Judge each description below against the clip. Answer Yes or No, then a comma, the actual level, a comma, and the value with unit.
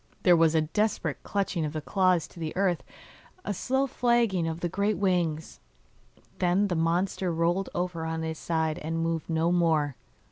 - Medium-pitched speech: Yes, medium, 170 Hz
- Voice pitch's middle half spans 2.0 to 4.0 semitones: Yes, average, 2.9 semitones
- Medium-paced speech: Yes, average, 175 wpm